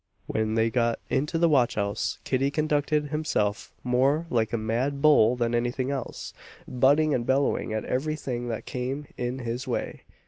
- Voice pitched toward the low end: Yes, low, 125 Hz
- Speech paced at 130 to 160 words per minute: No, average, 175 wpm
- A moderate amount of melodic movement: Yes, average, 3.4 semitones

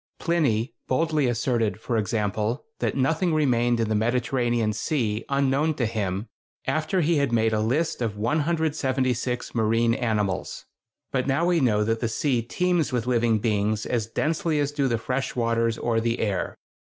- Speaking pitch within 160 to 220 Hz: No, low, 120 Hz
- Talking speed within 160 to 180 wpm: Yes, average, 165 wpm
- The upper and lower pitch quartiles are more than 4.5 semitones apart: No, average, 4.1 semitones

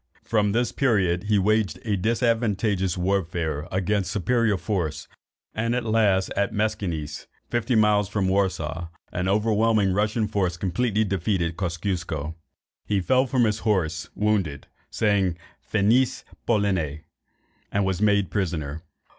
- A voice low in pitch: Yes, low, 100 Hz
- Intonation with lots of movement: No, average, 3.4 semitones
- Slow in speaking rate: Yes, slow, 130 wpm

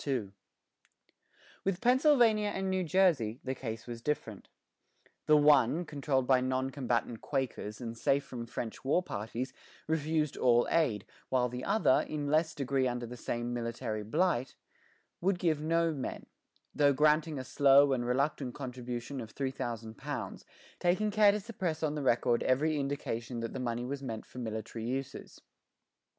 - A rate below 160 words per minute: Yes, average, 150 wpm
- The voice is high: No, low, 135 Hz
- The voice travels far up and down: No, average, 4.4 semitones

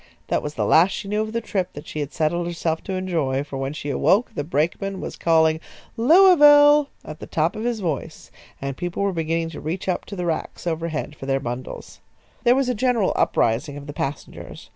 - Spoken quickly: Yes, fast, 215 wpm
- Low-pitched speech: No, medium, 165 Hz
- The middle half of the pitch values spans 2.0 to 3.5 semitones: No, wide, 5.6 semitones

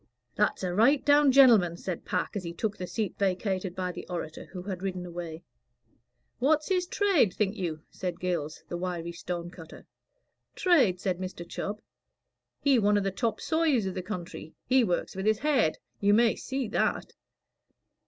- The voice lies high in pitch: Yes, high, 195 Hz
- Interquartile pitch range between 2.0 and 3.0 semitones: No, average, 4.9 semitones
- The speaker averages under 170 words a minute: No, average, 175 wpm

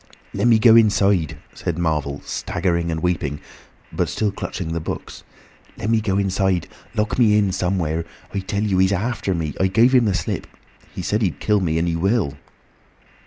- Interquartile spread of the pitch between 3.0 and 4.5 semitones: Yes, average, 3.8 semitones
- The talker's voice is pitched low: Yes, very low, 95 Hz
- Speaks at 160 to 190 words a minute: Yes, average, 170 wpm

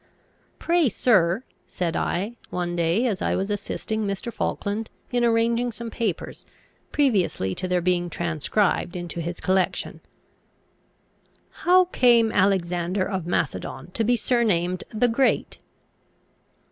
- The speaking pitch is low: No, high, 200 Hz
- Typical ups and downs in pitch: Yes, average, 5.0 semitones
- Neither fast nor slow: No, slow, 120 wpm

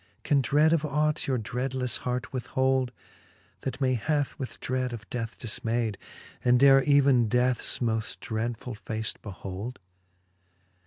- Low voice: Yes, low, 125 Hz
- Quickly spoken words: No, slow, 135 wpm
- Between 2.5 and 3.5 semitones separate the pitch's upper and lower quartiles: Yes, average, 2.9 semitones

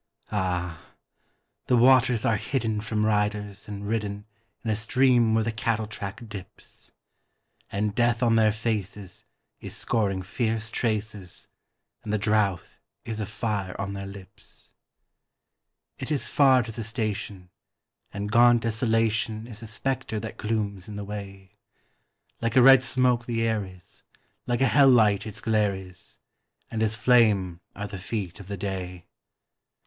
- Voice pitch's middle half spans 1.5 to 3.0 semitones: Yes, narrow, 2.4 semitones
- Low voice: Yes, low, 110 Hz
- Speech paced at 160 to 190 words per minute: No, average, 150 wpm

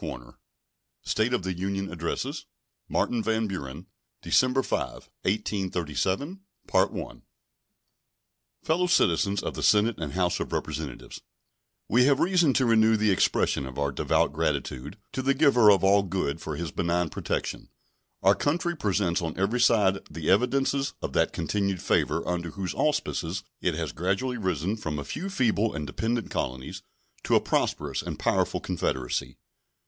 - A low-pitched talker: Yes, low, 100 Hz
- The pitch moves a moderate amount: No, wide, 6.1 semitones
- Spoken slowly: No, average, 145 wpm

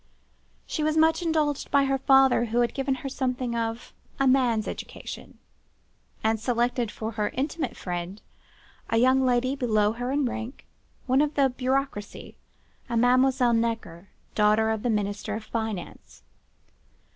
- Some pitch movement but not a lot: Yes, average, 3.3 semitones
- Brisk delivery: No, average, 145 wpm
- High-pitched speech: Yes, high, 245 Hz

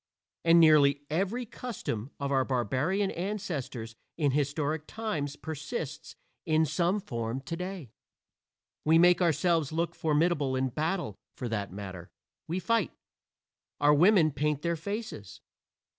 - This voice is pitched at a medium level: Yes, medium, 155 Hz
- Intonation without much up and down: No, average, 4.5 semitones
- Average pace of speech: No, slow, 125 wpm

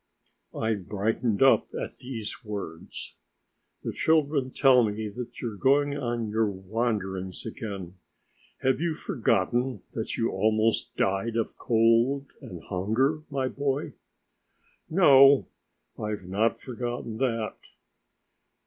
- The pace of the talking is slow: Yes, slow, 115 wpm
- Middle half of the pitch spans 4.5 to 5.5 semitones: No, average, 4.0 semitones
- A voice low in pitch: Yes, low, 115 Hz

